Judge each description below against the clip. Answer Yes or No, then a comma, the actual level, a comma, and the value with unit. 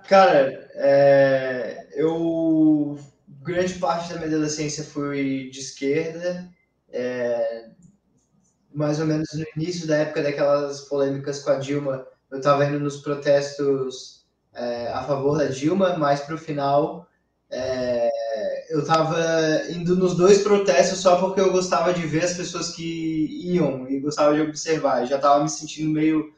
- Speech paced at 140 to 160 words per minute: Yes, average, 145 wpm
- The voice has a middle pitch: Yes, medium, 150 Hz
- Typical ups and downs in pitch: Yes, average, 3.1 semitones